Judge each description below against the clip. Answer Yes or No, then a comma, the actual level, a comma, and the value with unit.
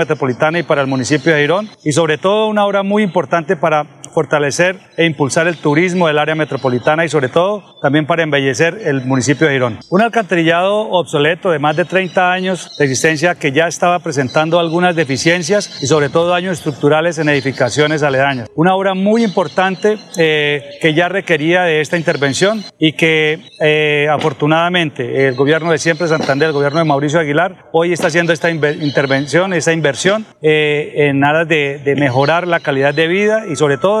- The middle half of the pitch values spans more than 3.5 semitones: No, average, 3.2 semitones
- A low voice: No, medium, 160 Hz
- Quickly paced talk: No, average, 180 wpm